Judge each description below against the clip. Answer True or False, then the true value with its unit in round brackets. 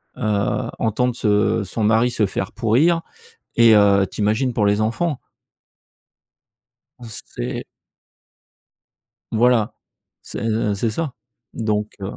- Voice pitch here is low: True (110 Hz)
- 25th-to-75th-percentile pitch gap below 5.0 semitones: True (2.4 semitones)